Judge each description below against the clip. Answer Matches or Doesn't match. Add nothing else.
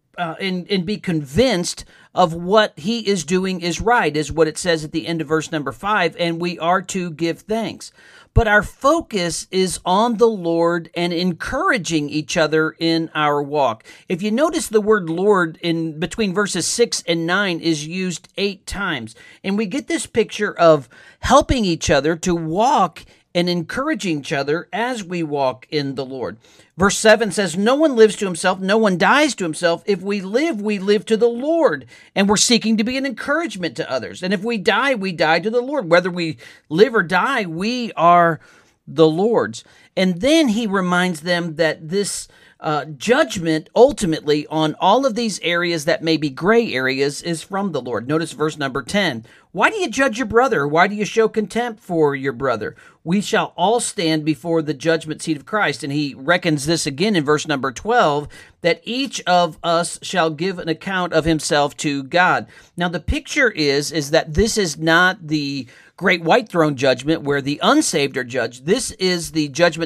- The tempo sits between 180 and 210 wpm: Matches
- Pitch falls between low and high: Matches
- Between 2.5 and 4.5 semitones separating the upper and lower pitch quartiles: Doesn't match